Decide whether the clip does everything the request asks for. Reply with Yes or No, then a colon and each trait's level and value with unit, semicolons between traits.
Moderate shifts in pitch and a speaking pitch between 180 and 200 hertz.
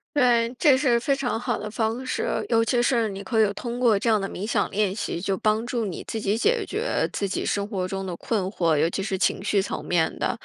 No: average, 3.6 semitones; high, 215 Hz